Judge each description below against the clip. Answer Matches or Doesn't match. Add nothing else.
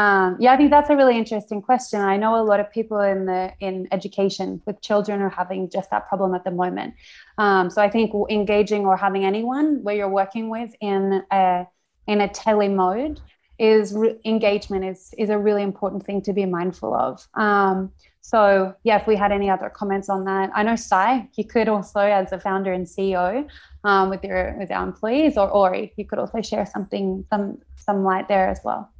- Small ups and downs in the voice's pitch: Matches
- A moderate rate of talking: Doesn't match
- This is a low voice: Doesn't match